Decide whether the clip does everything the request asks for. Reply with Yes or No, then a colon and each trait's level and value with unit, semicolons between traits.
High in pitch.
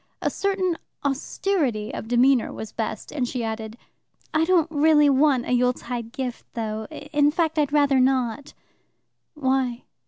Yes: very high, 265 Hz